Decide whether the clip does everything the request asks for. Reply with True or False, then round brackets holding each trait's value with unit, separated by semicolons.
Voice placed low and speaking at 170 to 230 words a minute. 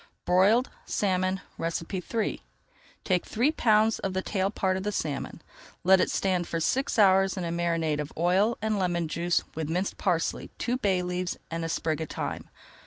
False (185 Hz; 175 wpm)